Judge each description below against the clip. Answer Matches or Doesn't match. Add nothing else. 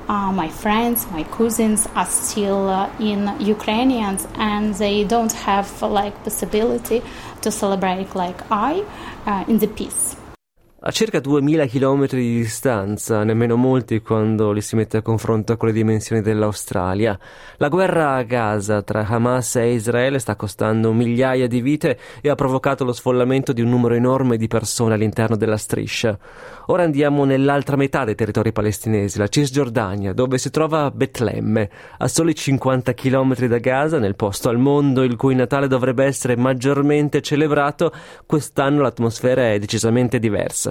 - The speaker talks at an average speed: Matches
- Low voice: Matches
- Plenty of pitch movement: Matches